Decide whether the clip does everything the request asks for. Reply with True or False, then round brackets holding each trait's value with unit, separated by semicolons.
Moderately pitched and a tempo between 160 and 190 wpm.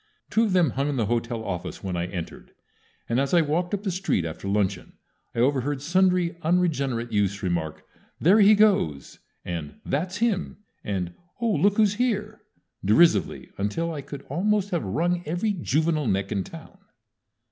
True (150 Hz; 170 wpm)